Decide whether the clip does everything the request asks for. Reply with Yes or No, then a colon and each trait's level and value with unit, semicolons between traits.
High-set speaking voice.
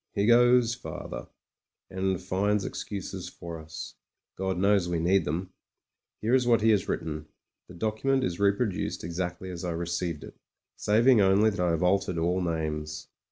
No: very low, 95 Hz